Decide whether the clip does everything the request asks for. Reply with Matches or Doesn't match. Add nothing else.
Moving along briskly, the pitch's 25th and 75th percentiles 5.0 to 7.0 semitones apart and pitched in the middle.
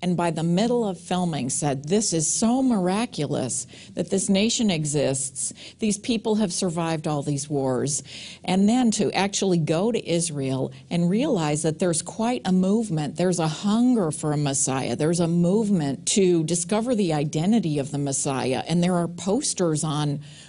Doesn't match